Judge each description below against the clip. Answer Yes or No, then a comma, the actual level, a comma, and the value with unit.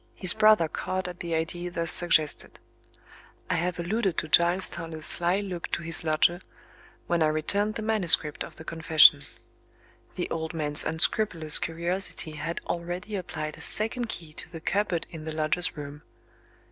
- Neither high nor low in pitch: Yes, medium, 170 Hz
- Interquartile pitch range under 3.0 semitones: Yes, narrow, 2.5 semitones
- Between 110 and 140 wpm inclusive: No, average, 160 wpm